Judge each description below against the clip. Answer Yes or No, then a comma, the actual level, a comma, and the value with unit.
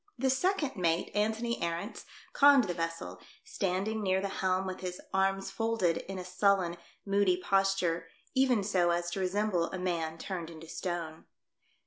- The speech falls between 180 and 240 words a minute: No, average, 155 wpm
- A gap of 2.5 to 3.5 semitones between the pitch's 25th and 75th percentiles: Yes, average, 3.1 semitones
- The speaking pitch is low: No, medium, 185 Hz